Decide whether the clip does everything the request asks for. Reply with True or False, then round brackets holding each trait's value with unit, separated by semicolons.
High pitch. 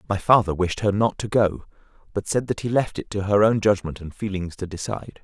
False (100 Hz)